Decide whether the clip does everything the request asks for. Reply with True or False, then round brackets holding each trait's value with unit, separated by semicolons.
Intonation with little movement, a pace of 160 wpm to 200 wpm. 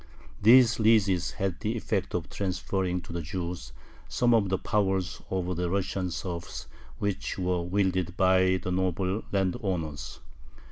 False (1.8 semitones; 140 wpm)